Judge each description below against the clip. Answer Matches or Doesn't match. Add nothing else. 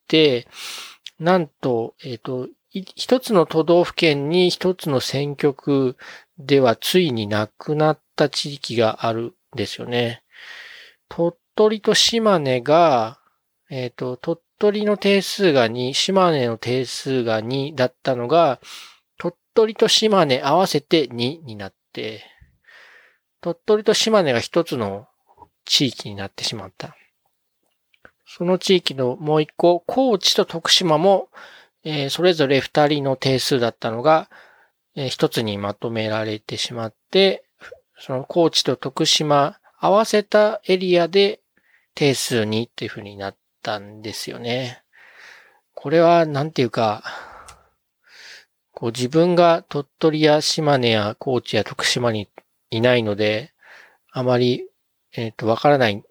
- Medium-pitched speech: Matches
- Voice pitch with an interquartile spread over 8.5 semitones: Doesn't match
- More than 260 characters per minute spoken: Doesn't match